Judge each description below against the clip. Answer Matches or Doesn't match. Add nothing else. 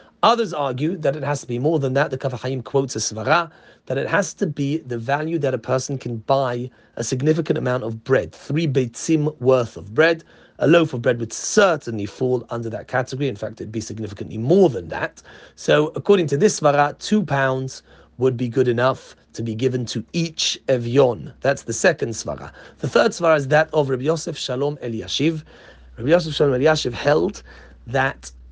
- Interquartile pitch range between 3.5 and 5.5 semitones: Matches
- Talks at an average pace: Matches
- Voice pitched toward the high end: Doesn't match